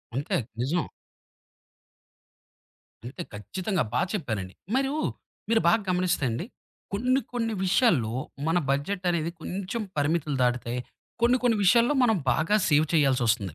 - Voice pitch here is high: No, medium, 170 Hz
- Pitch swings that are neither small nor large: No, wide, 8.2 semitones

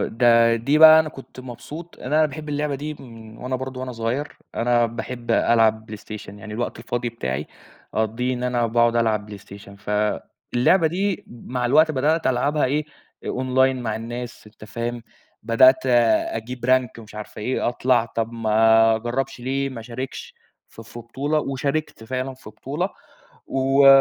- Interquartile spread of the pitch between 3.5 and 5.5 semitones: No, average, 3.0 semitones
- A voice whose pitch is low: Yes, low, 120 Hz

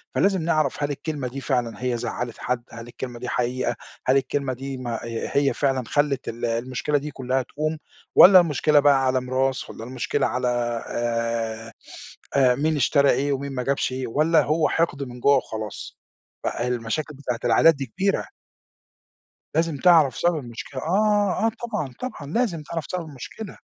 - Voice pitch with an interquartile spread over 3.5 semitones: Yes, average, 3.9 semitones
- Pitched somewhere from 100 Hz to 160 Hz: Yes, low, 135 Hz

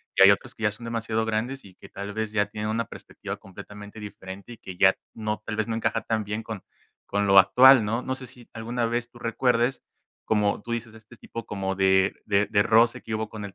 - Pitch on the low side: Yes, low, 110 Hz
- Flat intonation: Yes, narrow, 2.2 semitones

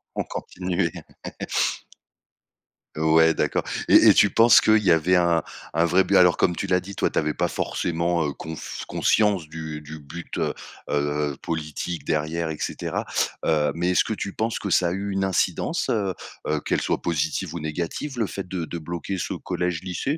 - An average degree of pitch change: Yes, average, 3.0 semitones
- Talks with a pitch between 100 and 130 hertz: No, very low, 85 Hz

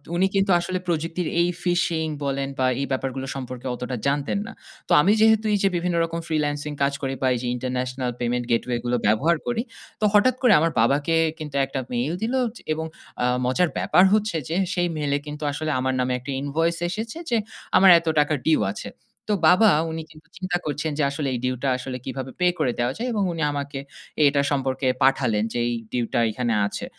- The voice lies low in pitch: No, medium, 145 Hz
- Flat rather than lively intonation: No, average, 5.0 semitones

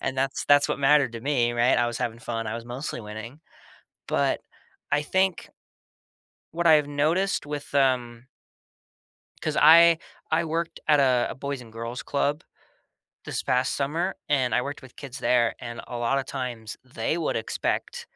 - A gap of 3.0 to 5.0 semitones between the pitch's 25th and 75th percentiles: Yes, average, 3.8 semitones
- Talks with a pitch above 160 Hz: No, low, 135 Hz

